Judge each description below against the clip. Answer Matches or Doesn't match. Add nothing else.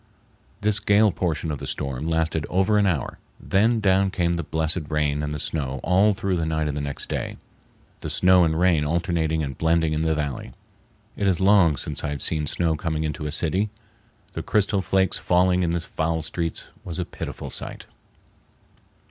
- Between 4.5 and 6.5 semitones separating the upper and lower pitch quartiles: Doesn't match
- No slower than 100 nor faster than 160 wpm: Doesn't match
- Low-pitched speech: Matches